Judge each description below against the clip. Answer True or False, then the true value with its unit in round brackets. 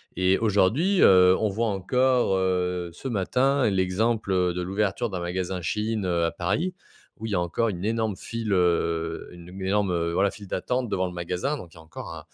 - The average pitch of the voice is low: True (95 Hz)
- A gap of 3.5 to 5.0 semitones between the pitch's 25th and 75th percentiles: True (3.9 semitones)